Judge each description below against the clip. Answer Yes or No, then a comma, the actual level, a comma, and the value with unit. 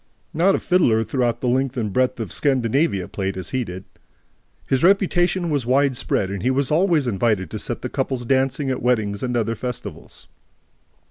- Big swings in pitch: No, average, 4.1 semitones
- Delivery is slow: No, average, 180 wpm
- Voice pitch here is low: Yes, low, 125 Hz